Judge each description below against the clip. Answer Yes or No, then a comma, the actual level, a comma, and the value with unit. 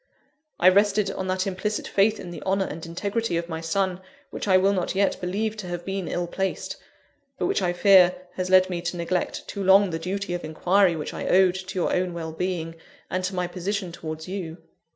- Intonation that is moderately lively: No, narrow, 2.0 semitones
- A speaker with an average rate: No, fast, 215 wpm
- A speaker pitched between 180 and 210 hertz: Yes, medium, 185 Hz